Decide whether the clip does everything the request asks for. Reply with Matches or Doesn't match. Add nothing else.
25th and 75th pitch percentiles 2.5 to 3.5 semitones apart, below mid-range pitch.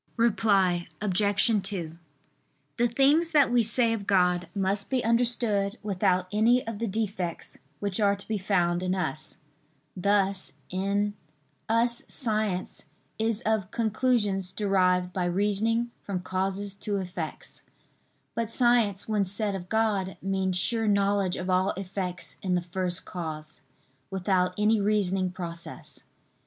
Doesn't match